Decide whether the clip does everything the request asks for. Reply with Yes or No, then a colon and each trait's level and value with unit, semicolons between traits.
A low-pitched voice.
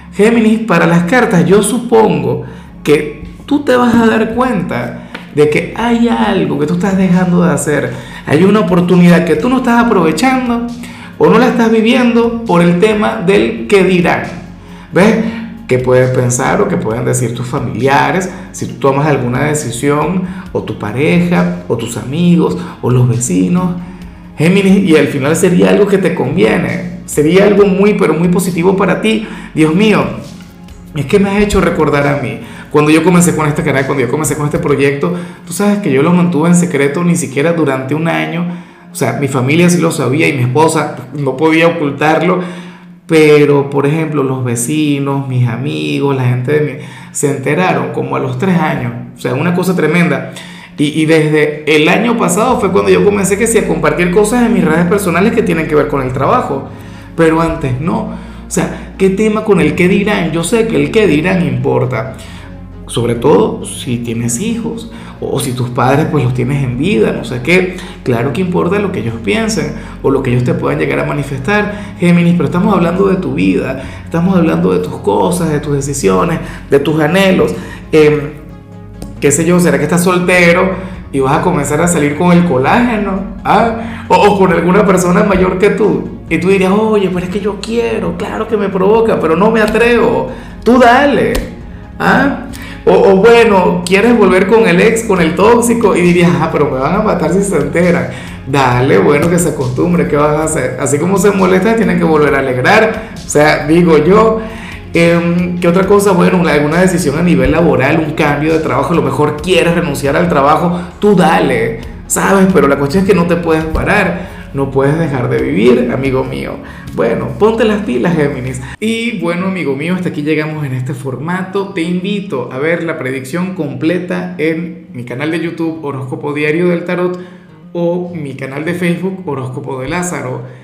No: medium, 170 Hz